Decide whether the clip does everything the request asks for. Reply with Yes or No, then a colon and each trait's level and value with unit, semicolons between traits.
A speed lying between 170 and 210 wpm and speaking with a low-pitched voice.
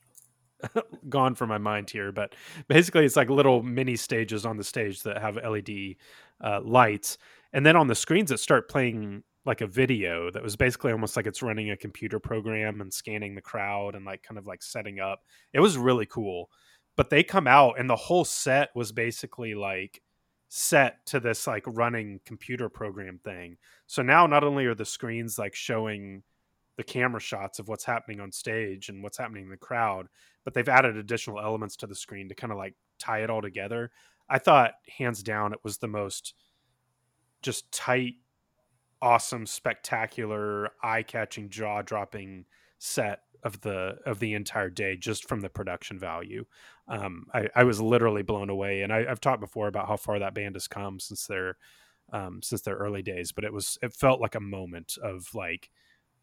Yes: average, 190 wpm; low, 110 Hz